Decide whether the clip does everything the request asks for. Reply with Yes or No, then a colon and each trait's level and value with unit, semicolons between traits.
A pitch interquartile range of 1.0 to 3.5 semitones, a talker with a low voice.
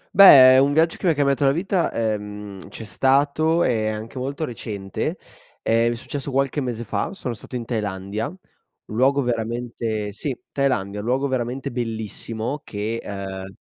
No: average, 4.3 semitones; low, 120 Hz